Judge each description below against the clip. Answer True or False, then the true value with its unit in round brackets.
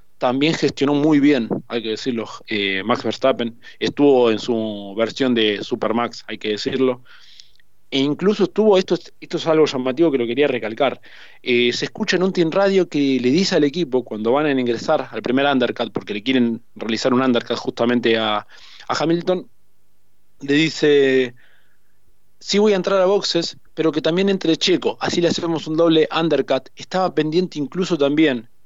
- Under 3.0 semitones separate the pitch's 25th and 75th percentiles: False (5.6 semitones)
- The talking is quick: False (175 wpm)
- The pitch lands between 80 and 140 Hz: True (135 Hz)